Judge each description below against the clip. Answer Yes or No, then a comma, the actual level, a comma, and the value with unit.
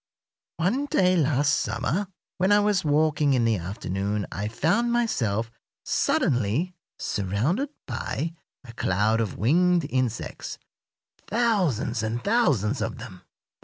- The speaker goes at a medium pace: No, slow, 120 wpm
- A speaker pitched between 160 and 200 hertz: No, low, 135 Hz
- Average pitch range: No, wide, 8.8 semitones